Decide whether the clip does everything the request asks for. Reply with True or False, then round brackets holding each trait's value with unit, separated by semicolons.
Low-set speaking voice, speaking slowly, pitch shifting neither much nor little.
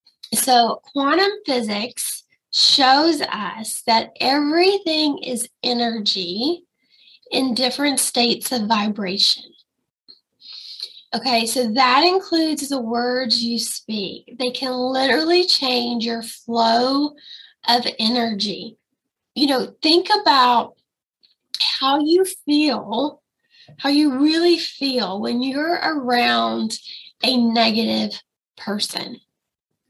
False (255 Hz; 95 wpm; 4.2 semitones)